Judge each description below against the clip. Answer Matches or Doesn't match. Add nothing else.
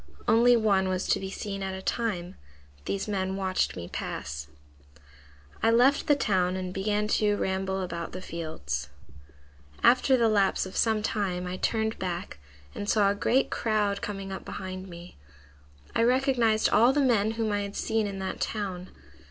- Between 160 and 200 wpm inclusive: Matches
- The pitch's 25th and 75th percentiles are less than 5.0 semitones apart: Matches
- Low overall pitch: Doesn't match